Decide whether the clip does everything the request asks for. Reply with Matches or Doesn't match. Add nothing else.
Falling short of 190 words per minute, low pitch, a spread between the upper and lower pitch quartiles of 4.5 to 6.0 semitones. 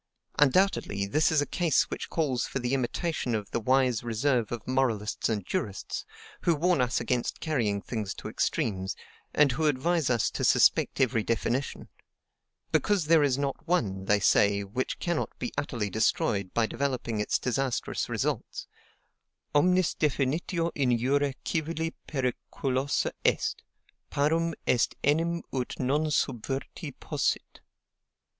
Matches